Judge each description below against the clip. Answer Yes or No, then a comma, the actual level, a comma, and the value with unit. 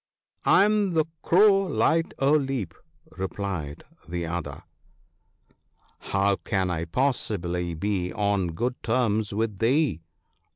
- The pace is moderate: No, slow, 125 wpm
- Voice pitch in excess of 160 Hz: No, low, 100 Hz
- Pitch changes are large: Yes, wide, 7.4 semitones